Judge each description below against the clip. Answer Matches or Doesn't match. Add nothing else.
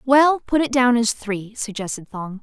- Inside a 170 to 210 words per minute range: Matches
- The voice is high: Matches